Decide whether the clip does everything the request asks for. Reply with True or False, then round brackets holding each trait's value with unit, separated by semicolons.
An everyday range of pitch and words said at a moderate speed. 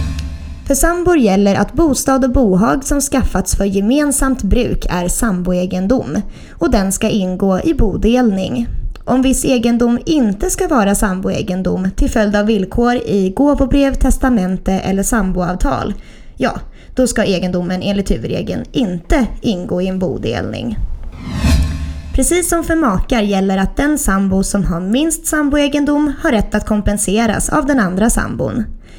False (6.1 semitones; 140 wpm)